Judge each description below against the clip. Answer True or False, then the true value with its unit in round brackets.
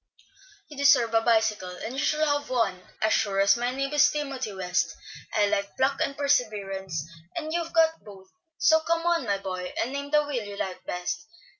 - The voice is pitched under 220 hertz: False (245 Hz)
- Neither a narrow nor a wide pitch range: False (6.6 semitones)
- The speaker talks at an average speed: True (195 wpm)